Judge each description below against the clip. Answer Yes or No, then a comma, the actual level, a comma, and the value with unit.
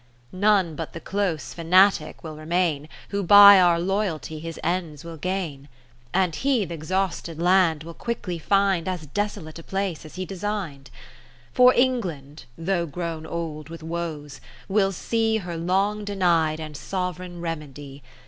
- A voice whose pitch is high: No, medium, 175 Hz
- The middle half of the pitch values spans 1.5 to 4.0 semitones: Yes, average, 3.5 semitones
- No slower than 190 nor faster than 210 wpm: No, average, 150 wpm